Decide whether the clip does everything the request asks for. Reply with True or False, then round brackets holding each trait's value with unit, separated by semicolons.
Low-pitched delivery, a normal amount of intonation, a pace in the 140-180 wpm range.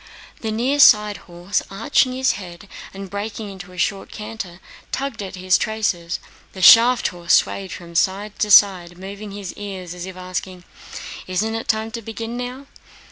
False (200 Hz; 3.4 semitones; 170 wpm)